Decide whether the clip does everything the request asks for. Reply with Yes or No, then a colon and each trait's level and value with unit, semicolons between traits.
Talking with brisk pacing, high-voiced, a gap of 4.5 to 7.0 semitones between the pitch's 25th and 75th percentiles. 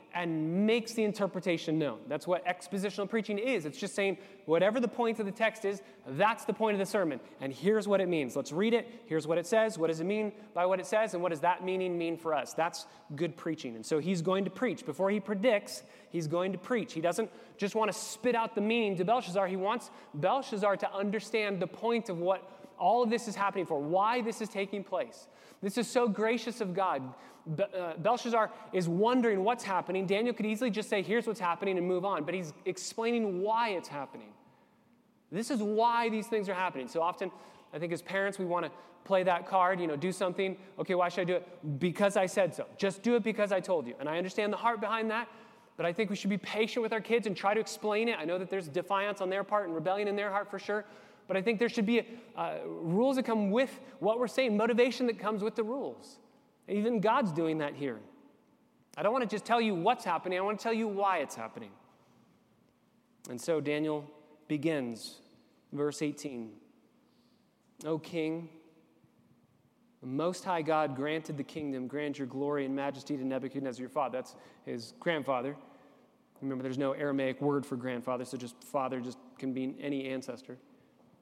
Yes: fast, 215 wpm; high, 195 Hz; average, 5.1 semitones